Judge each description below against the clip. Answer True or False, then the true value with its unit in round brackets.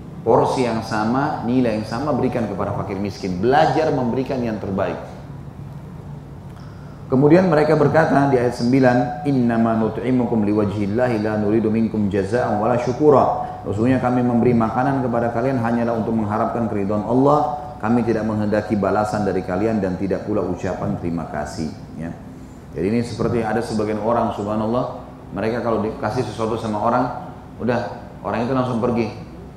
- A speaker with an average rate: True (145 wpm)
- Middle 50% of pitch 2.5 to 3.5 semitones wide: True (3.1 semitones)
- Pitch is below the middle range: True (115 Hz)